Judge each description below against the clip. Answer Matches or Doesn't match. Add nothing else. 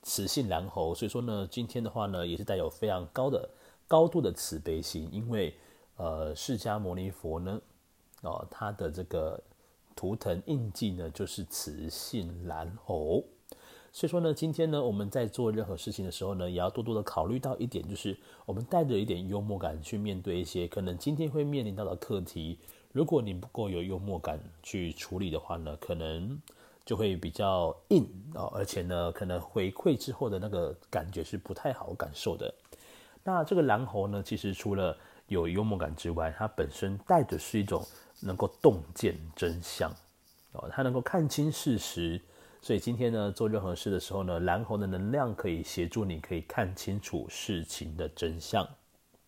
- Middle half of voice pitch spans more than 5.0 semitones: Matches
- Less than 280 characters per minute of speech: Matches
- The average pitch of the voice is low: Matches